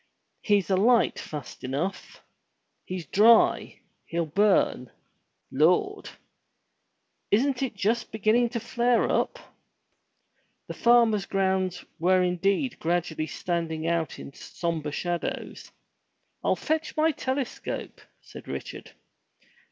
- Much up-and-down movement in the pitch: Yes, wide, 5.7 semitones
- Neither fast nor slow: No, slow, 100 wpm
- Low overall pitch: No, high, 190 Hz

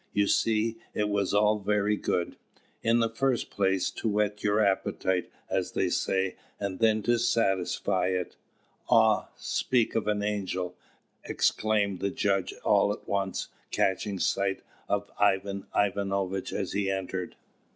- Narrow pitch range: Yes, narrow, 1.7 semitones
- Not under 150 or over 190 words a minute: No, average, 140 wpm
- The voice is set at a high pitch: No, low, 100 Hz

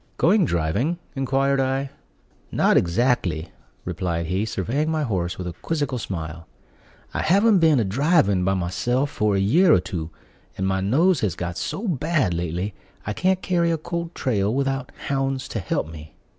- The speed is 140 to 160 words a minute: No, average, 170 wpm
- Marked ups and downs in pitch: Yes, wide, 8.8 semitones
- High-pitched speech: No, low, 120 Hz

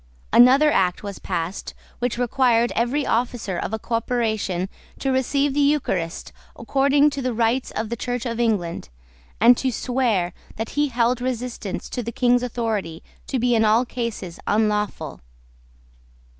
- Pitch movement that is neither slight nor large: Yes, average, 3.0 semitones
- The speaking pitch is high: Yes, high, 235 Hz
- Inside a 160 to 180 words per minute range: No, average, 150 wpm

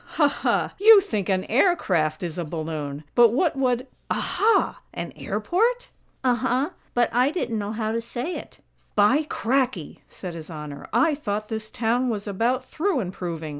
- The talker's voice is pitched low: No, high, 230 Hz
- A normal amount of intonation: No, wide, 6.7 semitones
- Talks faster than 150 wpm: Yes, average, 170 wpm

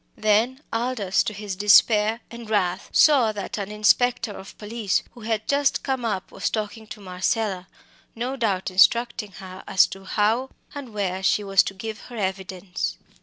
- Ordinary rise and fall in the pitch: Yes, average, 3.2 semitones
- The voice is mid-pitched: No, high, 210 Hz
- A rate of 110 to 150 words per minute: No, average, 170 wpm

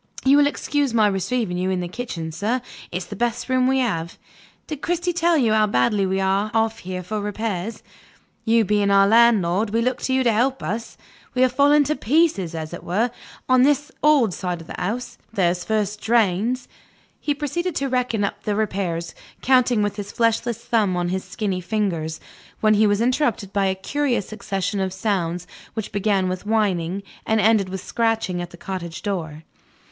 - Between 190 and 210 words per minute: Yes, average, 195 wpm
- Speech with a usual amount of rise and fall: Yes, average, 4.6 semitones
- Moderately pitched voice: No, high, 210 Hz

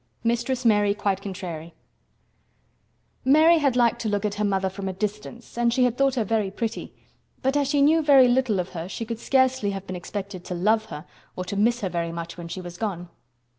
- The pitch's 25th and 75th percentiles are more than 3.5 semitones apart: Yes, average, 4.6 semitones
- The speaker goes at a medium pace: No, fast, 215 wpm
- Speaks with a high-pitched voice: Yes, high, 210 Hz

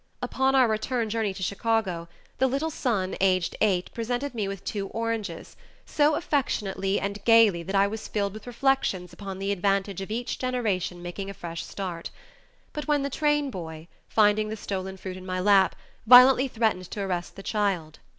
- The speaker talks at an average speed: Yes, average, 175 wpm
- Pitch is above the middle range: Yes, high, 205 Hz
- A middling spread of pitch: Yes, average, 3.9 semitones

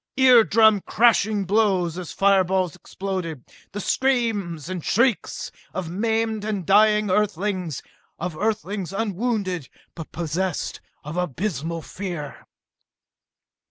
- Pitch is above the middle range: Yes, high, 195 Hz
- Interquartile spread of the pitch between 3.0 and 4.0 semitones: Yes, average, 3.7 semitones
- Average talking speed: No, slow, 105 wpm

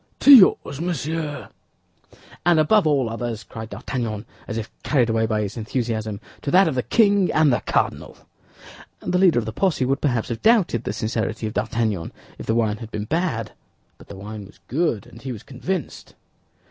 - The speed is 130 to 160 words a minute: No, average, 185 wpm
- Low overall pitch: Yes, low, 120 Hz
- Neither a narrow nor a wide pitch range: No, wide, 6.1 semitones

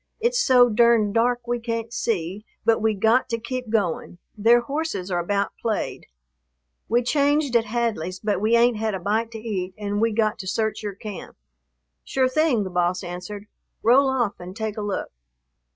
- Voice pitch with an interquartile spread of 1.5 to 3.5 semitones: Yes, average, 3.0 semitones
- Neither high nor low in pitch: No, high, 220 Hz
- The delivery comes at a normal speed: Yes, average, 185 wpm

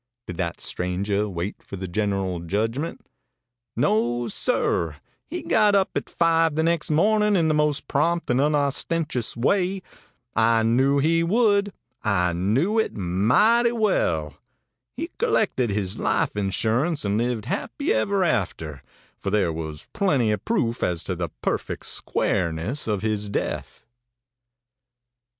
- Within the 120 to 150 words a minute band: Yes, slow, 135 wpm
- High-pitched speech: No, low, 115 Hz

